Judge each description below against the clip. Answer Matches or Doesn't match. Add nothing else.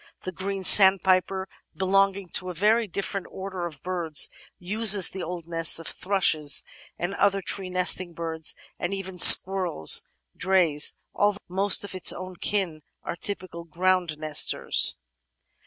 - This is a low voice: Doesn't match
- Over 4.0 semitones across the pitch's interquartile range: Doesn't match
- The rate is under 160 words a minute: Matches